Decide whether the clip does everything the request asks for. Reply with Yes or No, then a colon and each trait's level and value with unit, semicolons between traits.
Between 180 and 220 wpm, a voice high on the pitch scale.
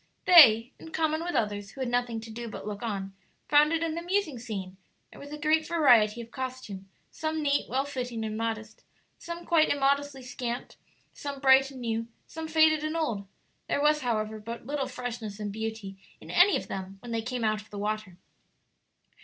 Yes: average, 195 wpm; high, 245 Hz